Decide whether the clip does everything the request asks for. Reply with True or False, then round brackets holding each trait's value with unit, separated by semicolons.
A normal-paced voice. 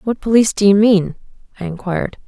True (185 wpm)